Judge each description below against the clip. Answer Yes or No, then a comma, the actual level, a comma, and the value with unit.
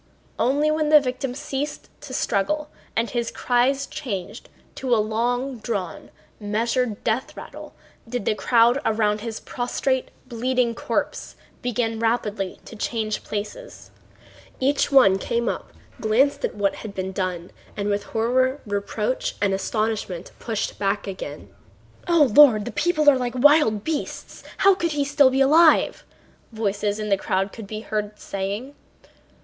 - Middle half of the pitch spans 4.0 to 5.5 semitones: Yes, average, 4.3 semitones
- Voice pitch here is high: Yes, high, 230 Hz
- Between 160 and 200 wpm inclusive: No, average, 145 wpm